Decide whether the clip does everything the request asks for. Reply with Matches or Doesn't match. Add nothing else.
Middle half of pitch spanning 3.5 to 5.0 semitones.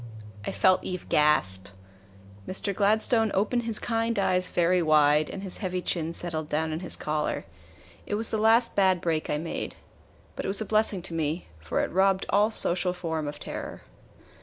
Matches